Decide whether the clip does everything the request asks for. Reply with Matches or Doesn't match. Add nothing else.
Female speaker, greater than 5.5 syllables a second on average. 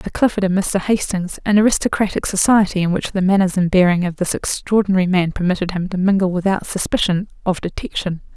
Matches